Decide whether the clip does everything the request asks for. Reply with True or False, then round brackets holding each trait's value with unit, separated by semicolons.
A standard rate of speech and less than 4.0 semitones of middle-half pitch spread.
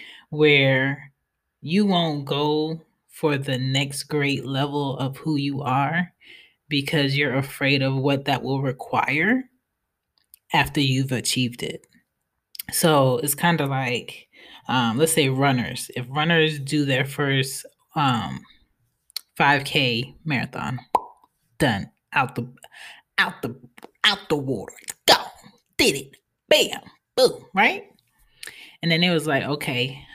False (125 wpm; 2.7 semitones)